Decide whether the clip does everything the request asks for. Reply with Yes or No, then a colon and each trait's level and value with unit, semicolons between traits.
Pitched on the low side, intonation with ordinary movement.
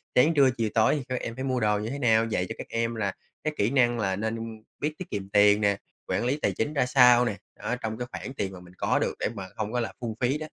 Yes: low, 115 Hz; average, 3.4 semitones